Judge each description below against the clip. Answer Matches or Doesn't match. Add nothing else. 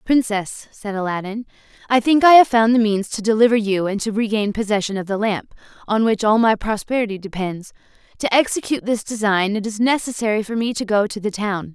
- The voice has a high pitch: Matches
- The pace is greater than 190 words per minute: Matches